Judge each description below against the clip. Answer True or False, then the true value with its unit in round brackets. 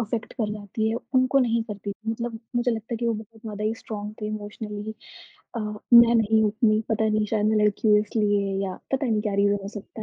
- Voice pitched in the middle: False (215 Hz)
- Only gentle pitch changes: True (1.4 semitones)